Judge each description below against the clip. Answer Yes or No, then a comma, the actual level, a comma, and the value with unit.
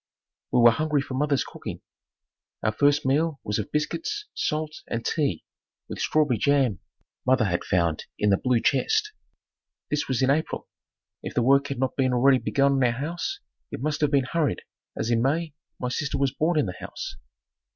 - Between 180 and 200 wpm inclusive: Yes, average, 185 wpm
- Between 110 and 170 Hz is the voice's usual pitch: Yes, medium, 140 Hz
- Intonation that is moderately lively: Yes, average, 3.7 semitones